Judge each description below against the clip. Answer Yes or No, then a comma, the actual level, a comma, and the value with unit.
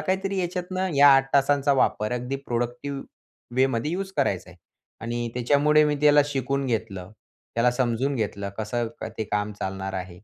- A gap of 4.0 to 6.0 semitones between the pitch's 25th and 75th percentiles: Yes, average, 4.6 semitones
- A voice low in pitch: Yes, low, 130 Hz